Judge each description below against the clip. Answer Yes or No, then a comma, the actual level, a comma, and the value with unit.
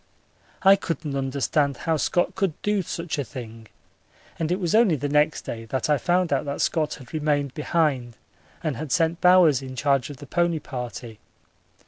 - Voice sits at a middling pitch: Yes, medium, 150 Hz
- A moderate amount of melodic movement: Yes, average, 4.1 semitones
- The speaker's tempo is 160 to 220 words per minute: Yes, average, 180 wpm